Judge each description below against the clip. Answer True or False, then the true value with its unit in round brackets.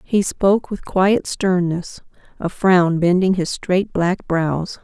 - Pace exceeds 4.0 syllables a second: False (3.4 syllables/s)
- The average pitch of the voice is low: False (180 Hz)